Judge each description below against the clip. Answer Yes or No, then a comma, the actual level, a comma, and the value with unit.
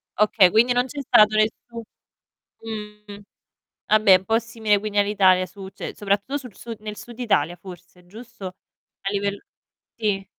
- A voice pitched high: Yes, high, 210 Hz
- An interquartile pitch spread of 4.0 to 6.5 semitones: No, average, 2.7 semitones